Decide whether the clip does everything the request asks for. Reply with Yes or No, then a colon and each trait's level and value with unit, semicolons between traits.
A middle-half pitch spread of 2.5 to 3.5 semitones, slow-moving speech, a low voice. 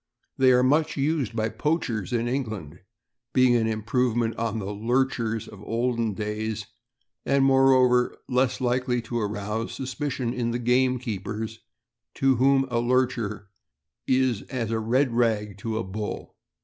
No: average, 2.8 semitones; average, 150 wpm; low, 120 Hz